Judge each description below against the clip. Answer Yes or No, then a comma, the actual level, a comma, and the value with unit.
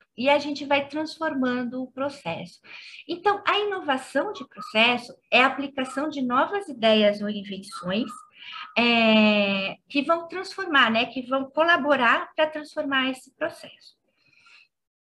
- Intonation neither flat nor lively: Yes, average, 4.9 semitones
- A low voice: No, very high, 270 Hz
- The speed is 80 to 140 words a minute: Yes, average, 130 wpm